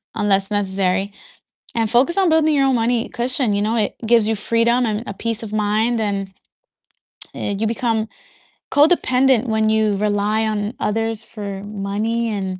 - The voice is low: No, high, 220 Hz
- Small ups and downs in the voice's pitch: Yes, narrow, 2.3 semitones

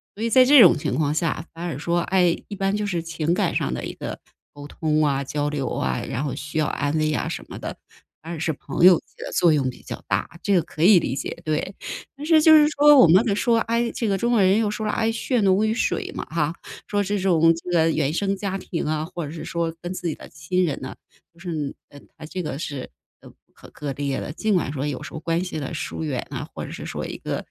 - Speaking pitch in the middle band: Yes, medium, 170 Hz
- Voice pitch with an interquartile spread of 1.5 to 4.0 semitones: No, average, 4.9 semitones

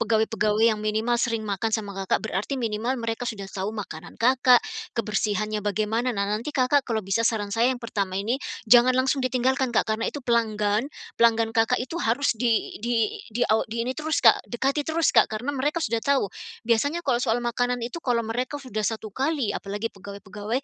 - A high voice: Yes, high, 230 Hz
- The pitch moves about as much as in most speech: Yes, average, 3.0 semitones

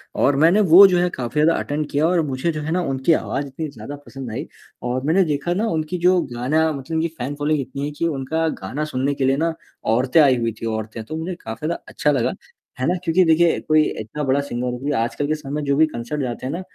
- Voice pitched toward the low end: No, medium, 145 Hz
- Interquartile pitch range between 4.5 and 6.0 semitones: No, average, 3.6 semitones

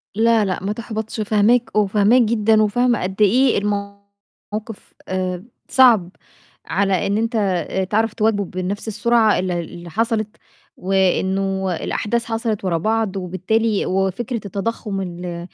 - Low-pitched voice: No, high, 205 Hz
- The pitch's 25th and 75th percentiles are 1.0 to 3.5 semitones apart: Yes, average, 2.8 semitones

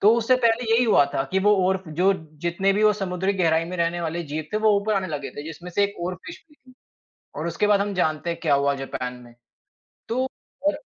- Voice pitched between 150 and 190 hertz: Yes, medium, 185 Hz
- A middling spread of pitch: Yes, average, 4.5 semitones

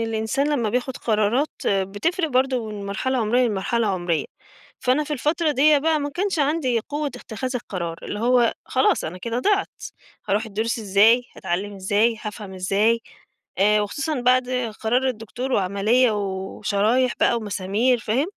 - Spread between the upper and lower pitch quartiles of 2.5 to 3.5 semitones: No, average, 4.2 semitones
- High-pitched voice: Yes, high, 230 Hz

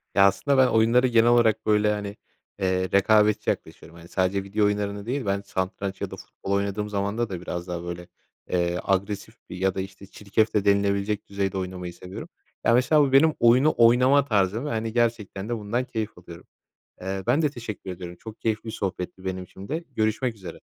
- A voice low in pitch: Yes, low, 100 Hz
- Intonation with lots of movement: No, average, 3.3 semitones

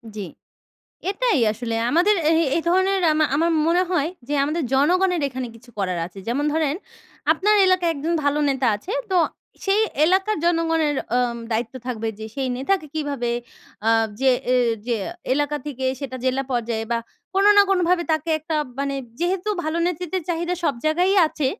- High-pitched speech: Yes, very high, 310 Hz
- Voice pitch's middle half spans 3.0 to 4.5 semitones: No, wide, 5.5 semitones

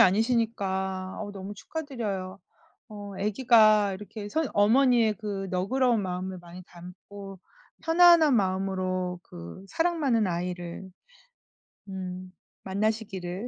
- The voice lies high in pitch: Yes, high, 200 Hz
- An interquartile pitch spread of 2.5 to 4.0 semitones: Yes, average, 3.4 semitones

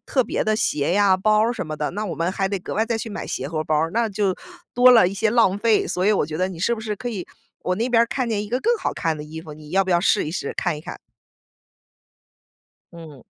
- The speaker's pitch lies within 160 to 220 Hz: Yes, high, 195 Hz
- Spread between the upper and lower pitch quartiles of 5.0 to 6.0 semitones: Yes, average, 5.3 semitones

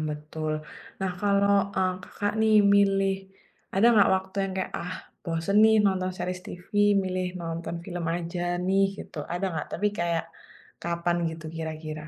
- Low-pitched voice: No, medium, 180 Hz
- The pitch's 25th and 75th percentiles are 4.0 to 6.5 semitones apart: No, average, 2.7 semitones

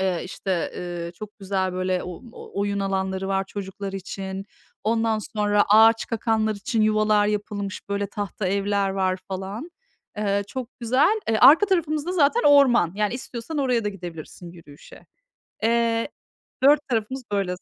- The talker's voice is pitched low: No, high, 205 Hz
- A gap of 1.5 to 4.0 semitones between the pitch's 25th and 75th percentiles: Yes, average, 3.1 semitones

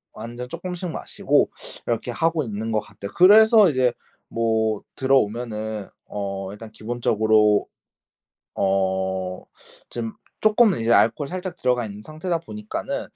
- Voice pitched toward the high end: No, low, 115 Hz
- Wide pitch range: Yes, wide, 7.6 semitones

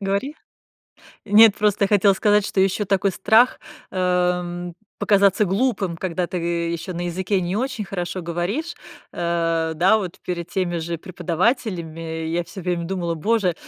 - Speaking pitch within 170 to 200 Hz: Yes, medium, 185 Hz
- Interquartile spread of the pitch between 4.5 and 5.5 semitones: No, average, 2.9 semitones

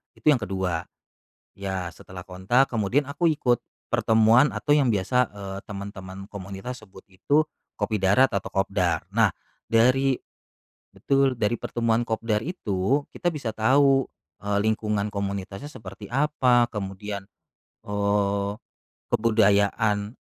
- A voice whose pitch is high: No, low, 105 Hz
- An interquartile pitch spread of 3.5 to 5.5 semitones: Yes, average, 4.2 semitones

